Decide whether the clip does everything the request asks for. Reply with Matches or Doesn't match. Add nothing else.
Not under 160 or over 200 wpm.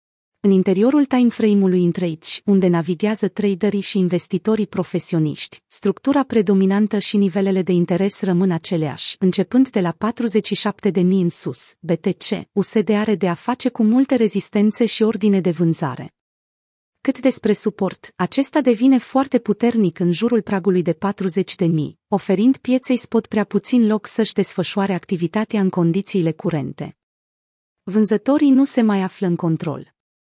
Doesn't match